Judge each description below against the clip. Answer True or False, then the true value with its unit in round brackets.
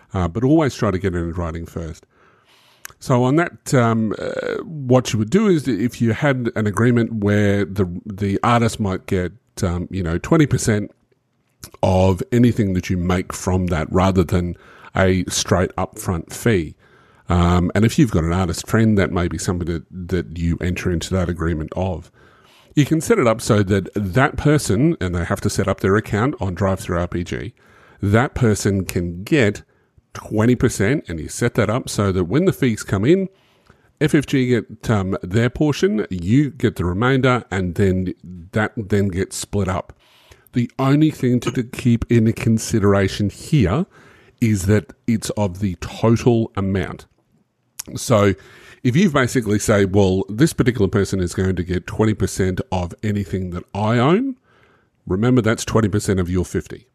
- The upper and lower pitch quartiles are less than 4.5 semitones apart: False (4.9 semitones)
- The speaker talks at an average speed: True (170 wpm)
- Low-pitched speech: True (105 Hz)